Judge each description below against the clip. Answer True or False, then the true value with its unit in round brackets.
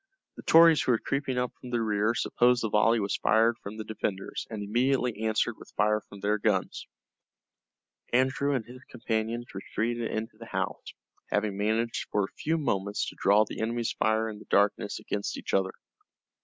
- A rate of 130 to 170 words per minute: False (185 wpm)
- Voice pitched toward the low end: True (110 Hz)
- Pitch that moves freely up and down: False (2.4 semitones)